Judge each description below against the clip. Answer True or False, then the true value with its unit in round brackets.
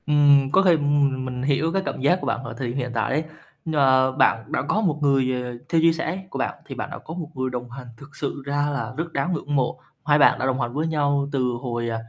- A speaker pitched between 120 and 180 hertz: True (140 Hz)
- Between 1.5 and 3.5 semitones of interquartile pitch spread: True (2.8 semitones)